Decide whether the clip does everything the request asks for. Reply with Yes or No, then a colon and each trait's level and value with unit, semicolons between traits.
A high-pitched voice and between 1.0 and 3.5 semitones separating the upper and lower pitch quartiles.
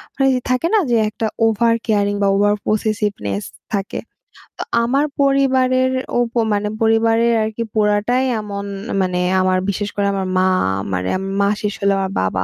Yes: high, 210 Hz; average, 2.8 semitones